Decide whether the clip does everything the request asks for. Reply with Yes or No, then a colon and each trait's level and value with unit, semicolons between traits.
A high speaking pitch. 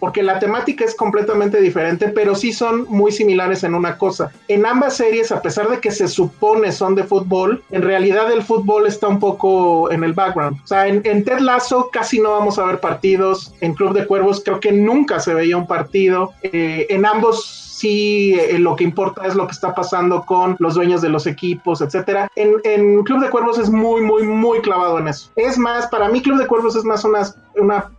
Yes: high, 200 Hz